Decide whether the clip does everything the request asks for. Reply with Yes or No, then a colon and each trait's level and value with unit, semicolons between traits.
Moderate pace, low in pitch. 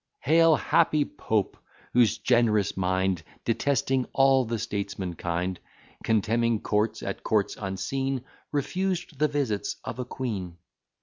No: slow, 120 wpm; low, 115 Hz